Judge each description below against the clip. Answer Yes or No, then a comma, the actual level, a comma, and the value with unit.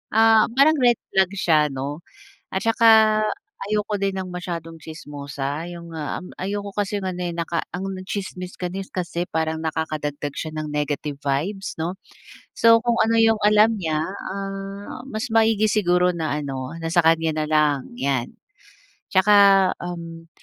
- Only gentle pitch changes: No, average, 4.8 semitones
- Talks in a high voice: No, medium, 180 Hz